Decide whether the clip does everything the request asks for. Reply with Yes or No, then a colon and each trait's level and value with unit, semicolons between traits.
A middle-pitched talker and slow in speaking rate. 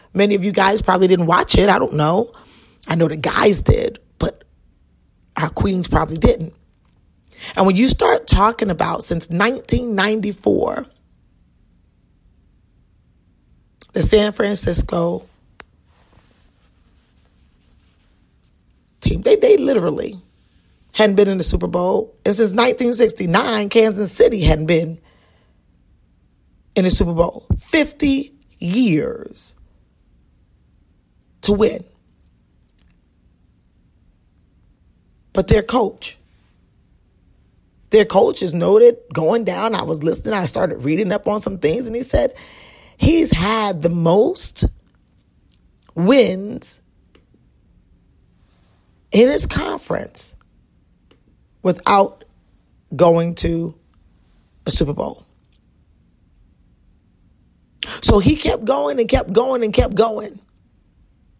No: high, 200 Hz; slow, 100 wpm